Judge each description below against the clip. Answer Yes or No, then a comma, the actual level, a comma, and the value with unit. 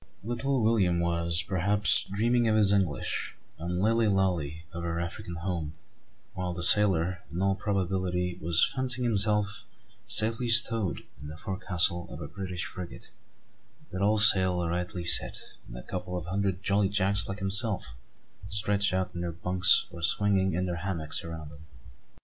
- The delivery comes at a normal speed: Yes, average, 160 wpm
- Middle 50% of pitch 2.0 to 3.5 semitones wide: Yes, average, 3.1 semitones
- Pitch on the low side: Yes, very low, 95 Hz